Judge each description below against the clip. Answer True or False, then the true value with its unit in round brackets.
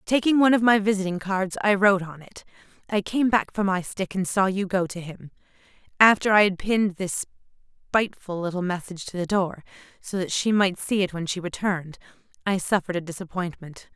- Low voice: False (190 Hz)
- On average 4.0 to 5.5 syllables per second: False (5.9 syllables/s)